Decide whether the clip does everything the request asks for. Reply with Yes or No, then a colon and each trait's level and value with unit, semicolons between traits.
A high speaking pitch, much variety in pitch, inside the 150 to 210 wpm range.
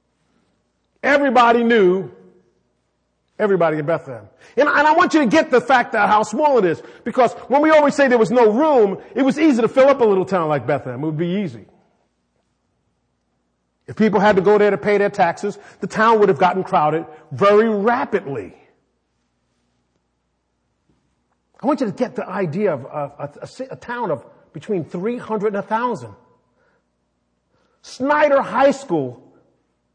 Yes: high, 200 Hz; wide, 8.7 semitones; average, 160 wpm